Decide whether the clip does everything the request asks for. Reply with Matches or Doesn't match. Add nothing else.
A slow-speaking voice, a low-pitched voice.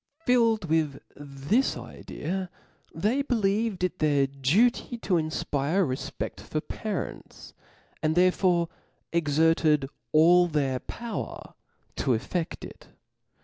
Doesn't match